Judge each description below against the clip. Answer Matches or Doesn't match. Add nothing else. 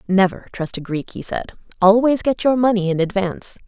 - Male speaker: Doesn't match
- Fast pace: Doesn't match